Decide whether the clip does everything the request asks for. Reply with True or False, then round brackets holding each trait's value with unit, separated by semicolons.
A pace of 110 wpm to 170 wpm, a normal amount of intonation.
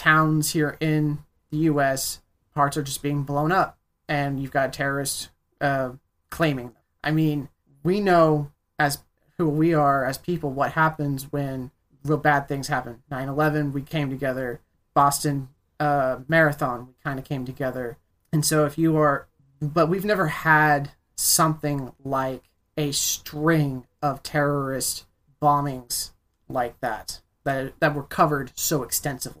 False (145 wpm; 2.1 semitones)